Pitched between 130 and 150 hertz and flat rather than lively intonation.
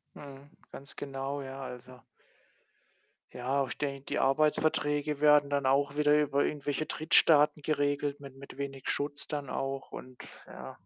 Yes: medium, 140 Hz; narrow, 1.4 semitones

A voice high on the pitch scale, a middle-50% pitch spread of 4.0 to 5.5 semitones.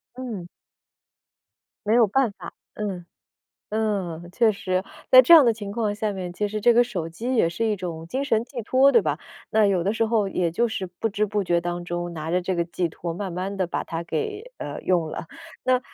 Yes: high, 200 Hz; average, 4.6 semitones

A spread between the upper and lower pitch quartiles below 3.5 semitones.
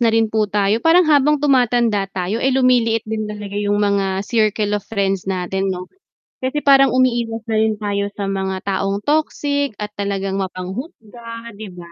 No: average, 3.8 semitones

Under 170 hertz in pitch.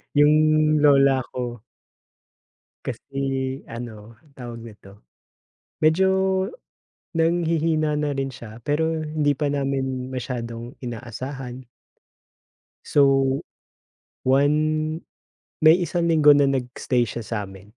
Yes: low, 135 Hz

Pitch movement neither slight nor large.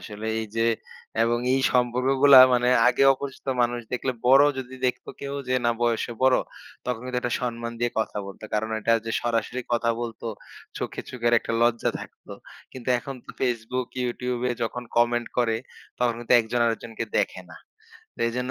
No: narrow, 1.5 semitones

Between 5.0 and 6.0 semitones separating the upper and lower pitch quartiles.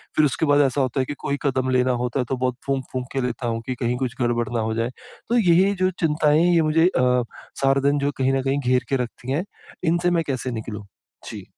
No: average, 3.1 semitones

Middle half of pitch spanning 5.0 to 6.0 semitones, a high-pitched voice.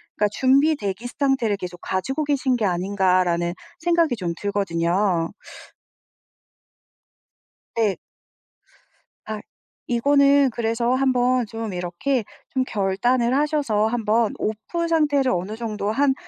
Yes: average, 5.3 semitones; high, 230 Hz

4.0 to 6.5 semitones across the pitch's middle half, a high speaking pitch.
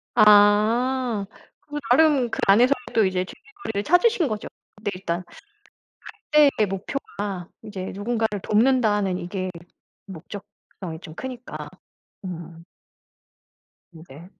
Yes: average, 5.2 semitones; high, 210 Hz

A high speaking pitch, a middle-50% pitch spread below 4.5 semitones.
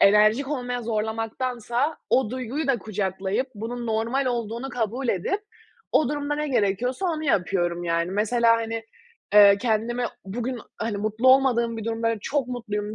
Yes: high, 230 Hz; average, 3.2 semitones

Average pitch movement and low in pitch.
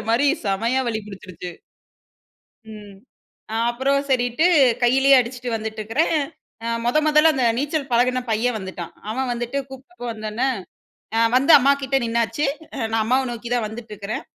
No: average, 3.5 semitones; high, 240 Hz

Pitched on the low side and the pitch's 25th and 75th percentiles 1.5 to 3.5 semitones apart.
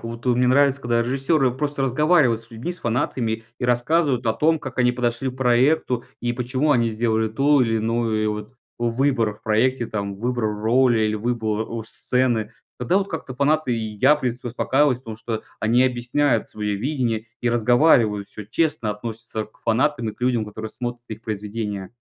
Yes: low, 120 Hz; average, 2.9 semitones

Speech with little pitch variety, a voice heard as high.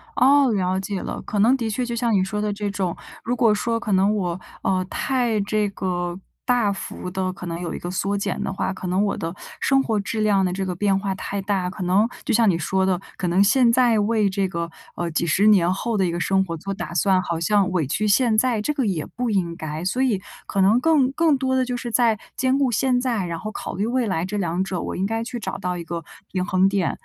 No: average, 3.9 semitones; high, 200 Hz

